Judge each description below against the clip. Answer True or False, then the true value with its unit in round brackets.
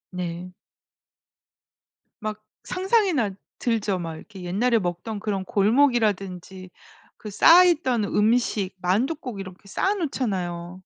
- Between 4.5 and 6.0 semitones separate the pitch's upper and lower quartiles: True (5.2 semitones)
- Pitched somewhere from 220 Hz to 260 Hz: False (210 Hz)